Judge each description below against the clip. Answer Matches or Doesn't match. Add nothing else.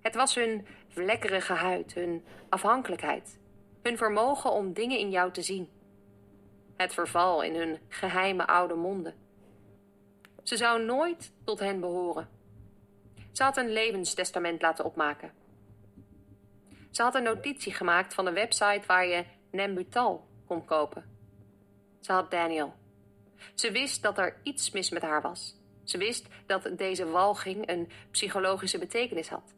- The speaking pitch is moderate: Matches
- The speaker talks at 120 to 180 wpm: Matches